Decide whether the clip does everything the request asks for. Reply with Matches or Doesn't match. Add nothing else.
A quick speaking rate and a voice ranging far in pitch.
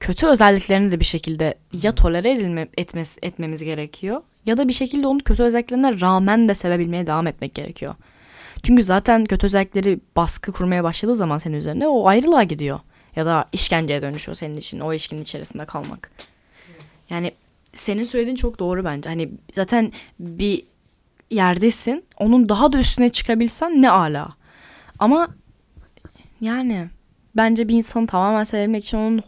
Matches